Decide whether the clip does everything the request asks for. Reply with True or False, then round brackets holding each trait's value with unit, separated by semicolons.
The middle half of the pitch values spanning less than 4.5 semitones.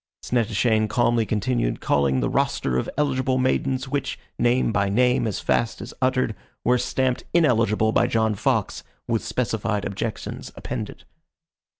True (3.1 semitones)